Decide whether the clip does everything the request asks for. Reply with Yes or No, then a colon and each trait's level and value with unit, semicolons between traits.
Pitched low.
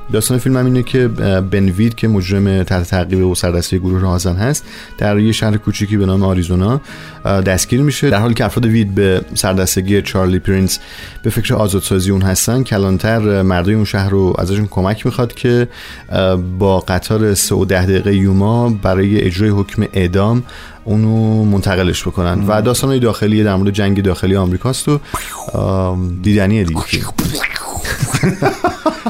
Yes: low, 100 Hz